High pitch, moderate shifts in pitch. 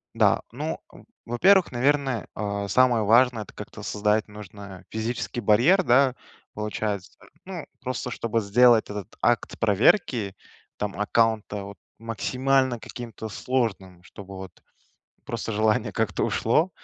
No: low, 110 Hz; average, 3.4 semitones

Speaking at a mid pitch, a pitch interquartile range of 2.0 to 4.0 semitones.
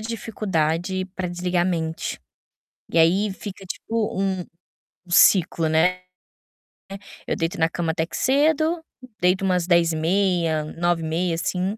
Yes: medium, 180 Hz; average, 2.9 semitones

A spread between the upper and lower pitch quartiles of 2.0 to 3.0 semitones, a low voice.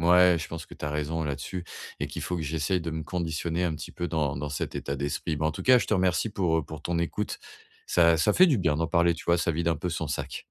Yes: narrow, 2.4 semitones; very low, 80 Hz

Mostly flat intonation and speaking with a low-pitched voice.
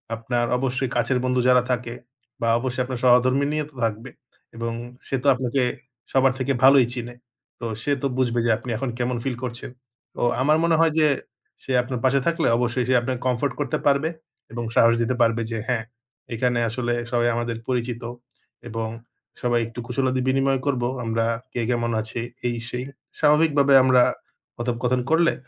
Yes: narrow, 2.1 semitones; low, 125 Hz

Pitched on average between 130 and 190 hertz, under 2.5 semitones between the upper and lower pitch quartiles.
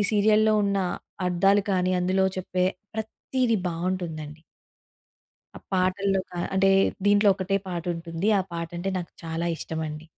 No: medium, 185 Hz; average, 2.9 semitones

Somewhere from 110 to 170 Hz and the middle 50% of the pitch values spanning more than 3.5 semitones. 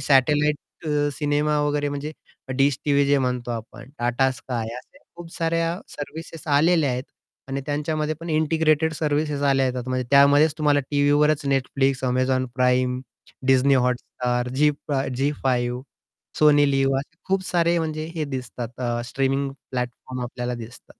No: medium, 140 Hz; average, 2.9 semitones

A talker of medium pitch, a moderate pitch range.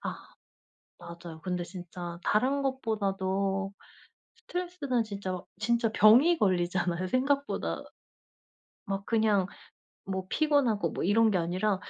No: high, 200 Hz; average, 4.6 semitones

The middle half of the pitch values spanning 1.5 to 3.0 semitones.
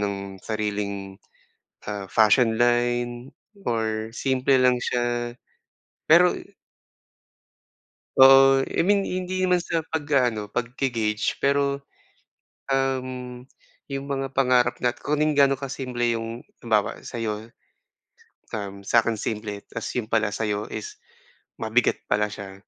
No: average, 3.7 semitones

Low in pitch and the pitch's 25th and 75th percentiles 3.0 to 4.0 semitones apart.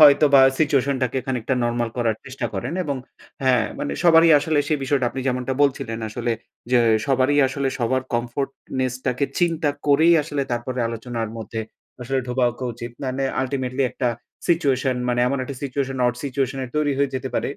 No: low, 130 Hz; narrow, 2.4 semitones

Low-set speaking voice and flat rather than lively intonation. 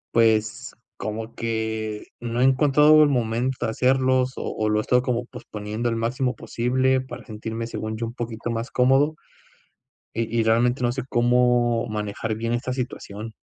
Yes: low, 120 Hz; narrow, 2.3 semitones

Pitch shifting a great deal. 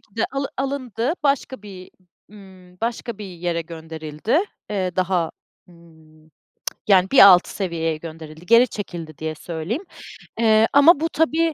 Yes: wide, 6.2 semitones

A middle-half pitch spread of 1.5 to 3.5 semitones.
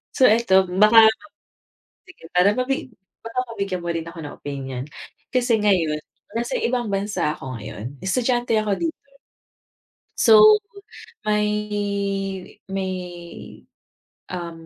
No: average, 4.8 semitones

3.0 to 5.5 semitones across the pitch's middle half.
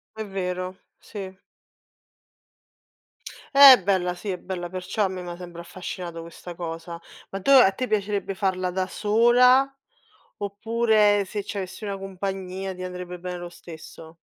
No: narrow, 2.4 semitones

